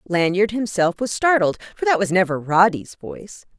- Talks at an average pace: Yes, average, 165 wpm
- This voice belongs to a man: No, female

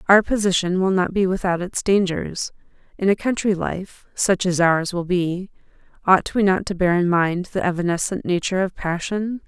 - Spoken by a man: No, female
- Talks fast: No, average, 185 wpm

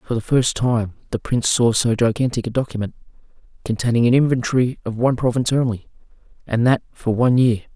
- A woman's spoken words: No, male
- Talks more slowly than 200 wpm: Yes, average, 180 wpm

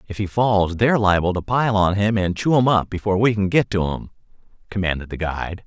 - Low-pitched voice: Yes, low, 100 Hz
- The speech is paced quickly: Yes, fast, 235 wpm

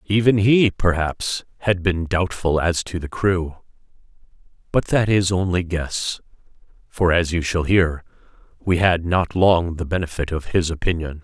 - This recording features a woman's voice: No, male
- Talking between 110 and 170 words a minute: Yes, average, 155 wpm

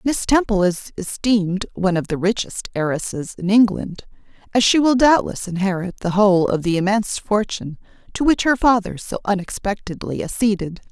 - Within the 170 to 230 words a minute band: No, average, 160 wpm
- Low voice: No, high, 200 Hz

